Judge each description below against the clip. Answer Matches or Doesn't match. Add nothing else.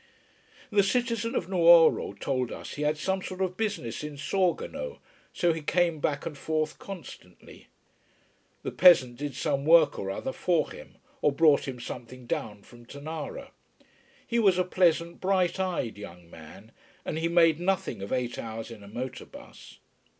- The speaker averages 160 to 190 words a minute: Matches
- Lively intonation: Matches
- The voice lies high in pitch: Doesn't match